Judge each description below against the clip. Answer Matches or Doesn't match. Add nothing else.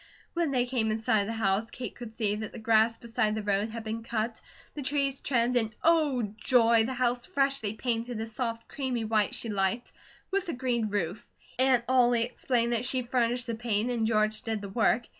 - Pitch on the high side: Matches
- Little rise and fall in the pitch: Matches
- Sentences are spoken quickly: Matches